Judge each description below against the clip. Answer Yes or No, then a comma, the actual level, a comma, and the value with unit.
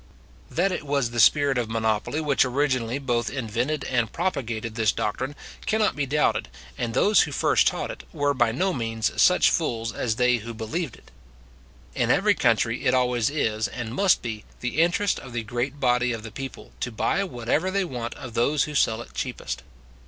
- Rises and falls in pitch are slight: No, average, 4.0 semitones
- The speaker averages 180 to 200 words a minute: Yes, average, 190 wpm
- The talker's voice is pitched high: No, low, 125 Hz